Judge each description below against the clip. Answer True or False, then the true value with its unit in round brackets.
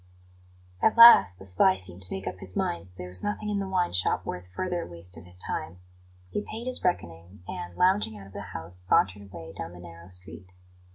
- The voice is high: False (90 Hz)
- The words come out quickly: True (220 wpm)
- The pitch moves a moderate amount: False (7.8 semitones)